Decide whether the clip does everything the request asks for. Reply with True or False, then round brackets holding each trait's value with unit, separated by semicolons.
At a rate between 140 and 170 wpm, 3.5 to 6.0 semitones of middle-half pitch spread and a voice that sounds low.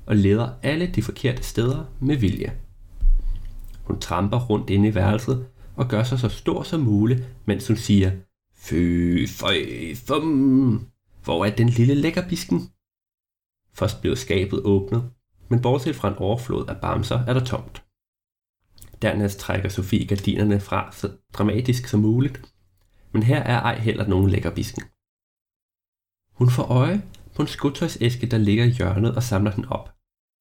True (150 wpm; 4.2 semitones; 105 Hz)